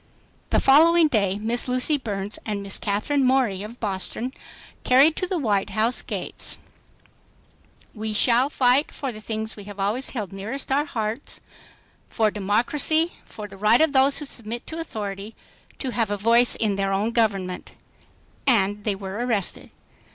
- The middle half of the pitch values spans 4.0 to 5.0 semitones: Yes, average, 4.4 semitones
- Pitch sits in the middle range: No, high, 225 Hz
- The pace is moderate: Yes, average, 160 wpm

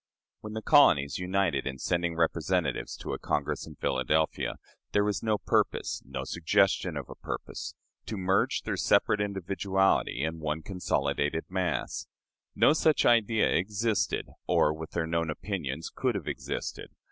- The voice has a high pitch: No, very low, 90 Hz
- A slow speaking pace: No, average, 145 wpm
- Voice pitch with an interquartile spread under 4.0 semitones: No, average, 4.4 semitones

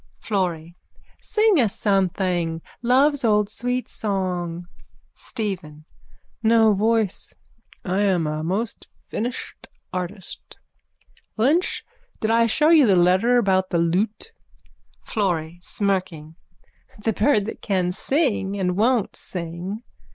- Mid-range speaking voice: No, high, 200 Hz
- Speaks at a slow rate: Yes, slow, 115 wpm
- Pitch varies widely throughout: No, average, 4.3 semitones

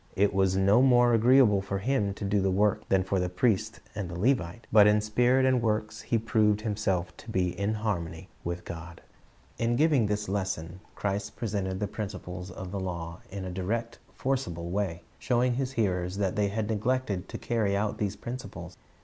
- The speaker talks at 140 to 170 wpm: No, average, 190 wpm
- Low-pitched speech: Yes, low, 100 Hz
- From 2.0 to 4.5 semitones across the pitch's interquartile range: Yes, average, 3.4 semitones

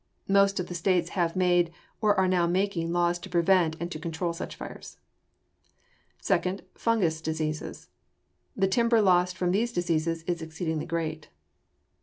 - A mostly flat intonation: Yes, narrow, 2.3 semitones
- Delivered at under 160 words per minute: Yes, average, 150 wpm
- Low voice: No, medium, 175 Hz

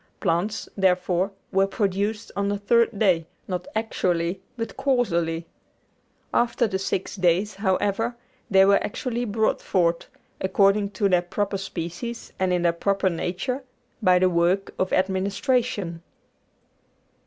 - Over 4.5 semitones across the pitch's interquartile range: No, average, 2.8 semitones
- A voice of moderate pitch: No, high, 195 Hz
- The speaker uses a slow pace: Yes, slow, 130 wpm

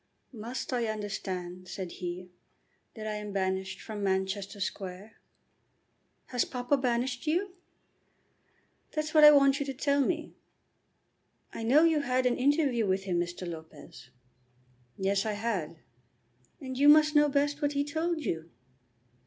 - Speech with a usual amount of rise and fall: No, wide, 7.0 semitones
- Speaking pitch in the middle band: No, high, 235 Hz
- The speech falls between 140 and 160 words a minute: Yes, average, 145 wpm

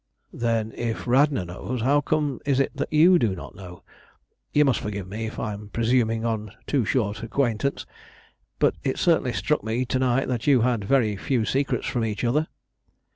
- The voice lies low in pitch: Yes, low, 120 Hz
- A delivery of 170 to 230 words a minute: Yes, average, 185 wpm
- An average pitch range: Yes, average, 3.9 semitones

